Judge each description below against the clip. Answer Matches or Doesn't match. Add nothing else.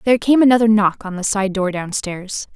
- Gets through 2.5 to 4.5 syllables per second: Doesn't match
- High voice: Matches